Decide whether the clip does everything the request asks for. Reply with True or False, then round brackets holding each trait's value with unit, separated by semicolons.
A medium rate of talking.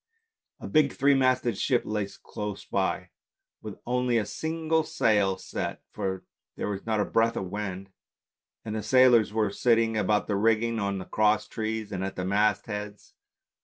True (170 wpm)